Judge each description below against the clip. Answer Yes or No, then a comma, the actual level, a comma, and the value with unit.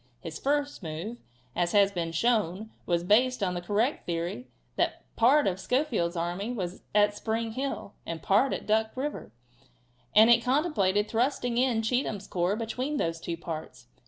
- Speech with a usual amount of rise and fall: No, wide, 5.9 semitones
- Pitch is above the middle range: Yes, high, 210 Hz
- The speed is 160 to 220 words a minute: Yes, average, 170 wpm